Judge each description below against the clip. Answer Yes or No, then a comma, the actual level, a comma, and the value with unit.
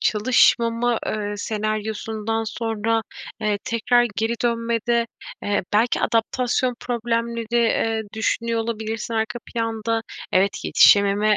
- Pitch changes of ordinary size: No, narrow, 1.4 semitones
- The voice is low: No, high, 225 Hz